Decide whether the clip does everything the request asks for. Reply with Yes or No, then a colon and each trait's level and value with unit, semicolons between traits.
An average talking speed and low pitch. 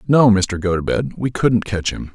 Yes: average, 195 wpm; low, 105 Hz